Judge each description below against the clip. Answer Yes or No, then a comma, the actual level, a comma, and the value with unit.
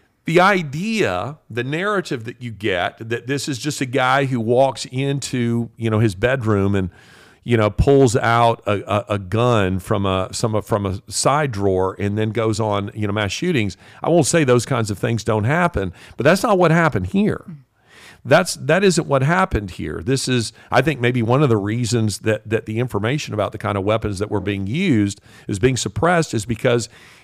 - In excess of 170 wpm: Yes, fast, 205 wpm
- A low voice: Yes, low, 115 Hz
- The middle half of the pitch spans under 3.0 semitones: No, average, 4.8 semitones